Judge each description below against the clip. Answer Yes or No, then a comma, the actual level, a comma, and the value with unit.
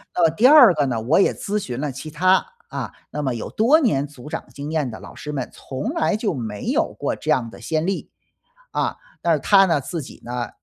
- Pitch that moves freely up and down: Yes, wide, 6.7 semitones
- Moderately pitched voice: Yes, medium, 150 Hz